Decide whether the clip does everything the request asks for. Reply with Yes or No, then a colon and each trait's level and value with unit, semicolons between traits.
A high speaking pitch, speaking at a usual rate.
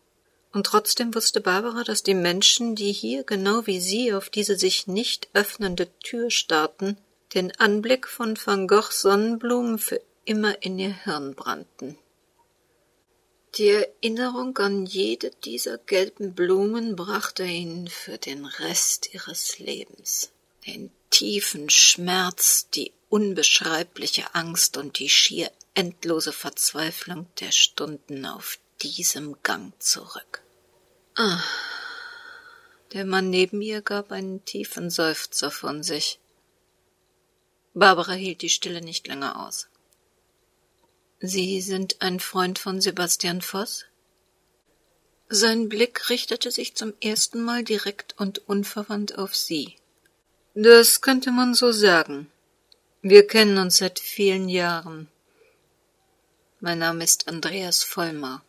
No: high, 195 Hz; slow, 120 wpm